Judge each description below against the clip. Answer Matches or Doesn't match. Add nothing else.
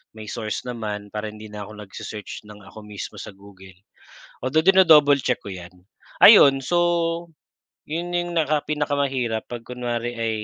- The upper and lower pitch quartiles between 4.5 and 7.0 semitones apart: Matches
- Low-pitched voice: Matches